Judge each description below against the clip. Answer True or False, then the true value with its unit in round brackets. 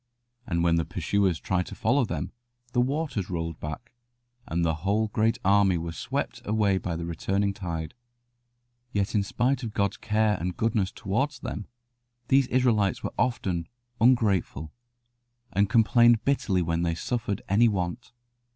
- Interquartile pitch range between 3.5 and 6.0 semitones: True (4.8 semitones)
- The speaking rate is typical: True (150 wpm)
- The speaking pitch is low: True (100 Hz)